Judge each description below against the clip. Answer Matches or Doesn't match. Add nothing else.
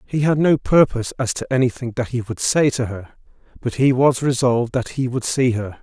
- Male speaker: Matches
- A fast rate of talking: Matches